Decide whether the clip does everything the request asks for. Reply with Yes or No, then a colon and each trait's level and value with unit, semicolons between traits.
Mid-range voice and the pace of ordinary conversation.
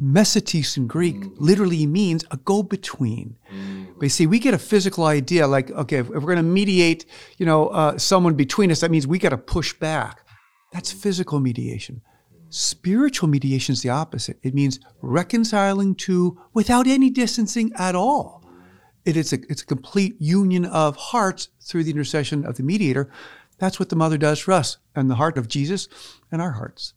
Yes: medium, 160 Hz; average, 185 wpm